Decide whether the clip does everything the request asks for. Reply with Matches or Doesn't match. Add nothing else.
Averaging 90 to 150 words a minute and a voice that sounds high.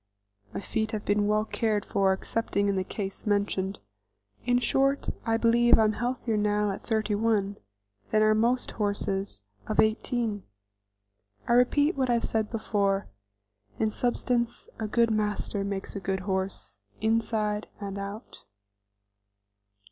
Matches